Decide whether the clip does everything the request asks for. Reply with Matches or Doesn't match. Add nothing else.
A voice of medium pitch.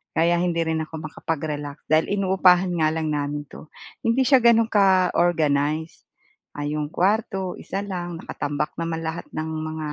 Matches